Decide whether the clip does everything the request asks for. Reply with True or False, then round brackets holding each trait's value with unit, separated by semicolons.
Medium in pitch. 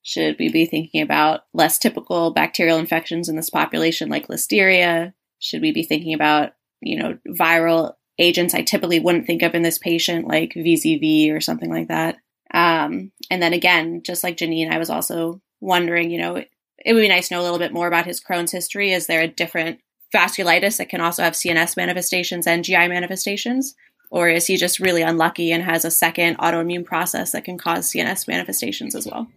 True (170 Hz)